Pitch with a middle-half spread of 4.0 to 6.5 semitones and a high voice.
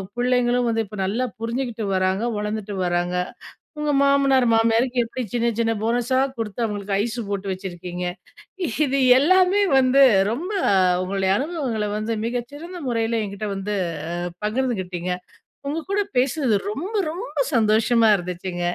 Yes: average, 4.4 semitones; high, 230 Hz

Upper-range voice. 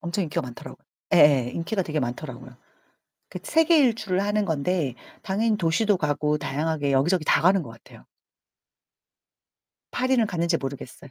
No: medium, 165 Hz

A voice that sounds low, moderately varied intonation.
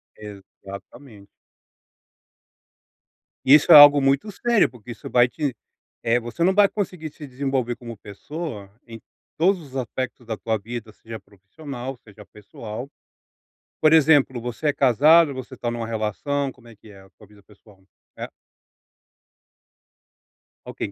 Yes: low, 125 Hz; average, 5.0 semitones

